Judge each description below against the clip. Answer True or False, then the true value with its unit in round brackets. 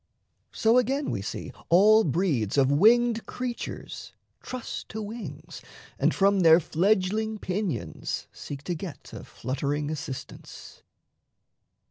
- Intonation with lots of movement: True (6.9 semitones)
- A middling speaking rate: False (115 wpm)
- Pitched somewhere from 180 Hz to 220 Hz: True (190 Hz)